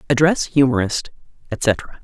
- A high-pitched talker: No, low, 135 Hz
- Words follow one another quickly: No, slow, 90 wpm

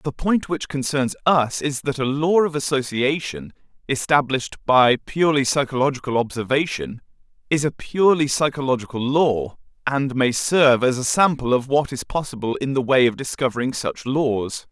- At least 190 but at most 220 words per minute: No, average, 155 wpm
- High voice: No, low, 135 Hz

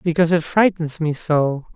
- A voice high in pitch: No, medium, 160 Hz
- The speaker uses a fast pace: No, average, 170 wpm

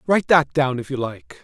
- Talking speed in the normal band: No, fast, 250 wpm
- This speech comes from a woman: No, male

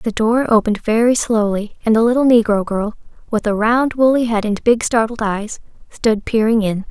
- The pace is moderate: Yes, average, 190 wpm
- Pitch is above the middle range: Yes, high, 225 Hz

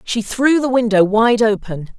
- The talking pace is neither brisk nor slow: Yes, average, 180 wpm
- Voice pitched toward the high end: Yes, high, 225 Hz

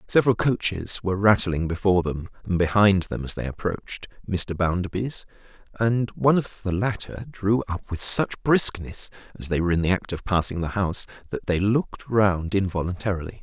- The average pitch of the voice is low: Yes, very low, 95 Hz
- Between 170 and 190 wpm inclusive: Yes, average, 175 wpm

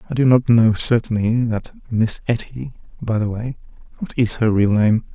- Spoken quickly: No, average, 175 wpm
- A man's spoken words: Yes, male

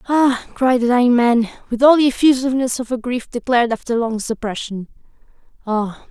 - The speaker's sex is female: Yes, female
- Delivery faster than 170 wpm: No, average, 165 wpm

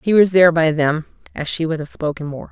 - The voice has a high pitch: No, medium, 160 Hz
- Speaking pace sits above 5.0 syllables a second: Yes, 6.1 syllables/s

